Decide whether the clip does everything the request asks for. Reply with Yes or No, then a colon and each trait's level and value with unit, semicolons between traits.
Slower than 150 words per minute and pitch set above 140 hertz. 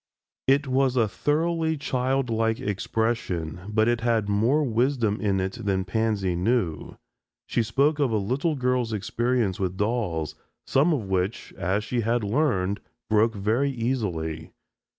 No: average, 140 wpm; low, 115 Hz